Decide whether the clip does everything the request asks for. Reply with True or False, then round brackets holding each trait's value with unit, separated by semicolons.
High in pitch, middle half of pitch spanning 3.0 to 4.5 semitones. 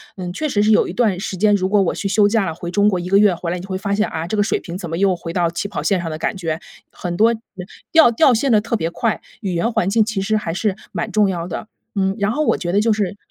True (200 Hz; 3.4 semitones)